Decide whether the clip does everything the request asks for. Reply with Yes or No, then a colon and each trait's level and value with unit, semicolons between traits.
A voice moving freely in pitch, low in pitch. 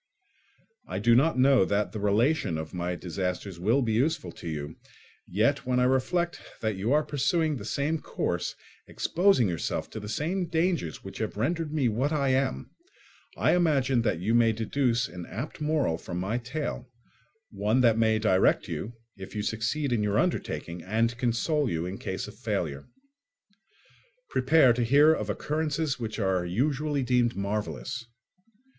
Yes: wide, 6.0 semitones; low, 120 Hz